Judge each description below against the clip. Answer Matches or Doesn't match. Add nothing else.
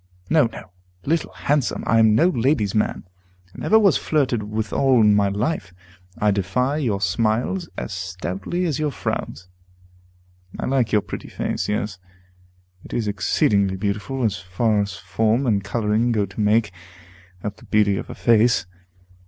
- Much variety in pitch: Doesn't match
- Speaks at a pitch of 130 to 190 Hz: Doesn't match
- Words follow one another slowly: Doesn't match